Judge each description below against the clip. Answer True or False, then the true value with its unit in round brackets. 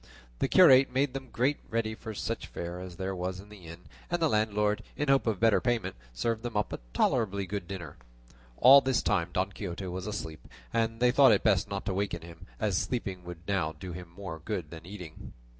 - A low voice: True (100 Hz)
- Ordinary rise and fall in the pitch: True (4.4 semitones)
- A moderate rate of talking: False (210 wpm)